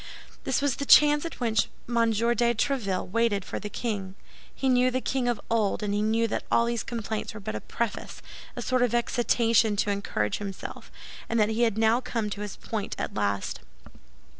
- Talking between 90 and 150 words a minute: No, average, 190 wpm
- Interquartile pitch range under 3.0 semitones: Yes, narrow, 2.6 semitones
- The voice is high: Yes, high, 225 Hz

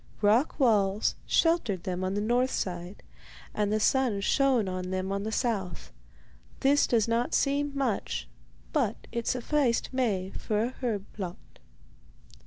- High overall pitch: Yes, high, 220 Hz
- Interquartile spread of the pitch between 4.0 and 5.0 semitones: Yes, average, 4.7 semitones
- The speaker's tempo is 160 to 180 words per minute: No, average, 145 wpm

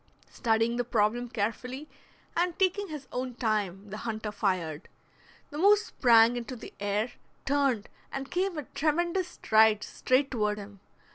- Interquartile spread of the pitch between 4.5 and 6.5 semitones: Yes, average, 5.3 semitones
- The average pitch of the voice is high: Yes, high, 240 Hz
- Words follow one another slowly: No, average, 145 wpm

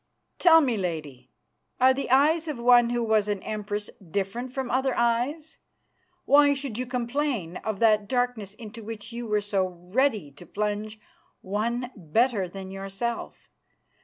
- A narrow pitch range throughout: No, average, 4.0 semitones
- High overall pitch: Yes, high, 225 Hz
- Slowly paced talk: No, average, 150 wpm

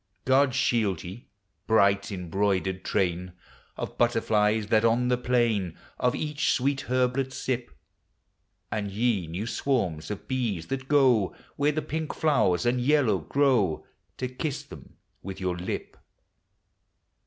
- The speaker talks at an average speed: No, slow, 130 wpm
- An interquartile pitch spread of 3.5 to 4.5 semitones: No, average, 5.1 semitones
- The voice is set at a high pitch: No, low, 115 Hz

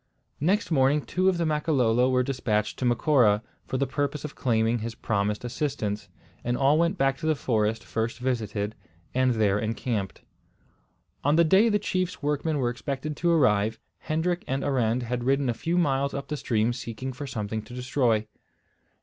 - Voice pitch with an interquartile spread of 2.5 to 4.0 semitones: No, average, 4.8 semitones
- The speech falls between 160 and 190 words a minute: Yes, average, 175 wpm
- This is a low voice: Yes, low, 130 Hz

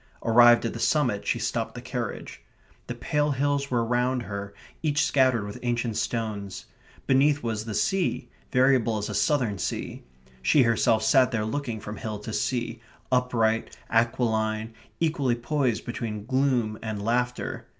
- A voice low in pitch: Yes, low, 120 Hz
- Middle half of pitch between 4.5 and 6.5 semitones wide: No, average, 2.9 semitones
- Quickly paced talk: No, average, 150 wpm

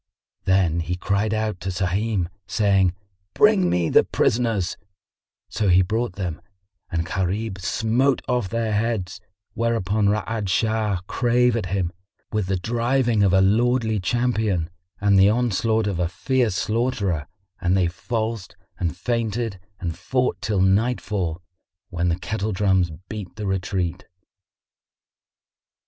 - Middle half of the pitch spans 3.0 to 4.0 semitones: Yes, average, 3.7 semitones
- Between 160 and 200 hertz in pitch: No, low, 100 Hz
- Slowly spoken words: Yes, slow, 130 wpm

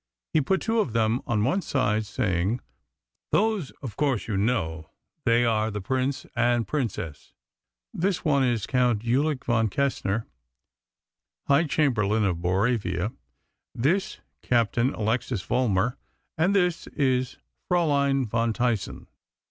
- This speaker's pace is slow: Yes, slow, 125 wpm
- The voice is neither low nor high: No, low, 120 Hz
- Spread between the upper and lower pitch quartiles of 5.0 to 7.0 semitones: No, average, 4.5 semitones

